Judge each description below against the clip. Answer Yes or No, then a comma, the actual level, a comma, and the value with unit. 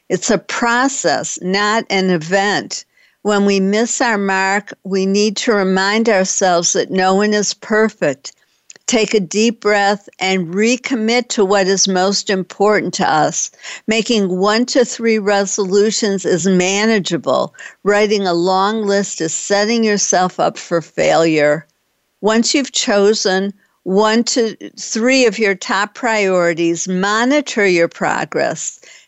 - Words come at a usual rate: No, slow, 130 wpm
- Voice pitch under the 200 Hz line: No, high, 205 Hz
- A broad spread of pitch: No, average, 2.7 semitones